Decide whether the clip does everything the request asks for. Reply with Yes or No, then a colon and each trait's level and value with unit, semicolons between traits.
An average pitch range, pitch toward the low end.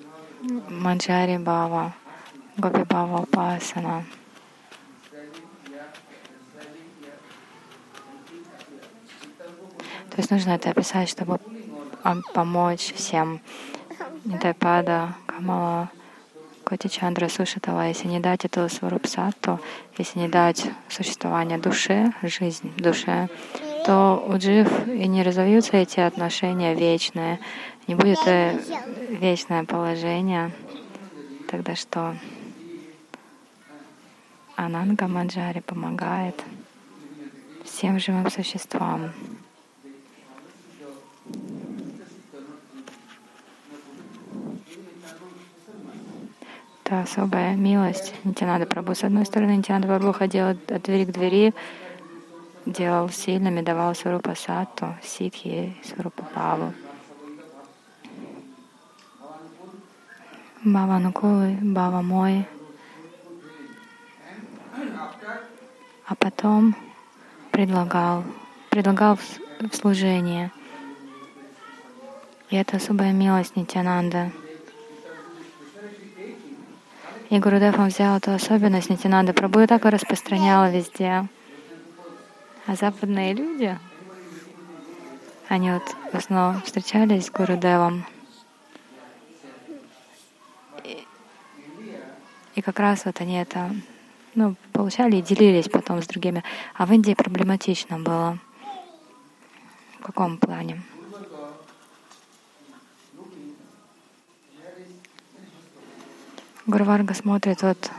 No: average, 4.0 semitones; high, 190 Hz